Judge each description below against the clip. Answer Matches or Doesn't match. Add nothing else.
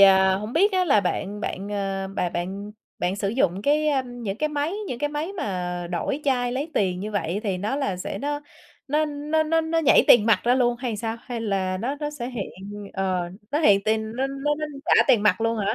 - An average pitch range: Doesn't match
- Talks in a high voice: Matches